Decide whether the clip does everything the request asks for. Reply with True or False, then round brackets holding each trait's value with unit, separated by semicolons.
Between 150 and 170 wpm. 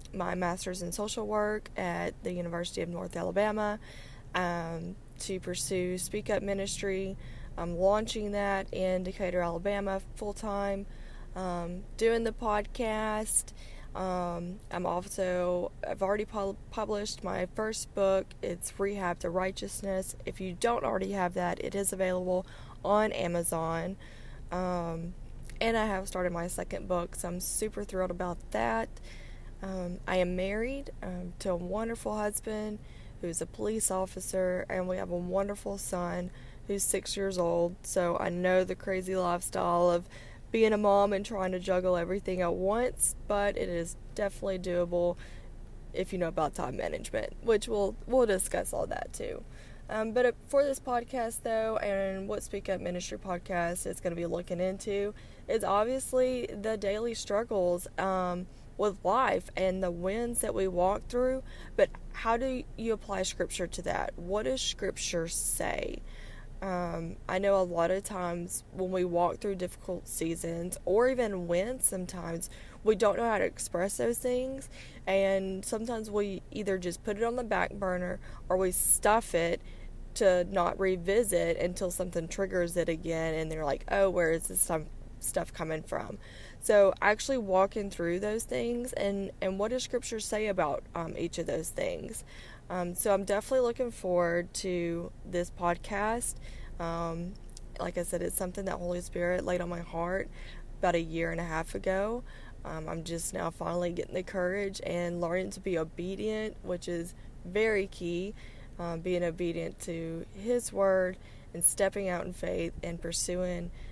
True (160 wpm)